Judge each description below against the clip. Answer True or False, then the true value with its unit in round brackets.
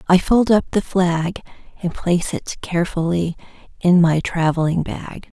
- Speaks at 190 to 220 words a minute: False (145 wpm)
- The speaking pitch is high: False (175 Hz)